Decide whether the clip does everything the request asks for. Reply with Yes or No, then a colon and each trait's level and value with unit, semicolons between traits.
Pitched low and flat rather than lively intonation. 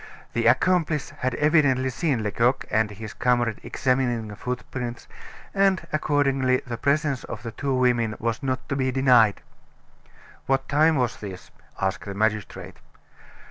No: low, 125 Hz; average, 3.5 semitones